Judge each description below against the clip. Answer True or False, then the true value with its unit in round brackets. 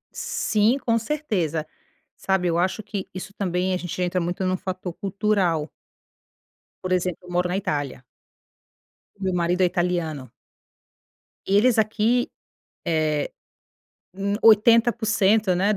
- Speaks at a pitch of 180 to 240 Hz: True (185 Hz)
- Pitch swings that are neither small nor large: True (3.1 semitones)